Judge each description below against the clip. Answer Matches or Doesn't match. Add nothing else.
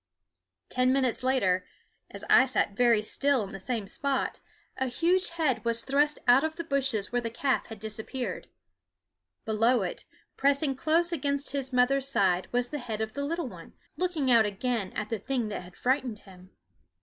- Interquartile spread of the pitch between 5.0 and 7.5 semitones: Doesn't match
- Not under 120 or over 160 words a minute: Doesn't match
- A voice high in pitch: Matches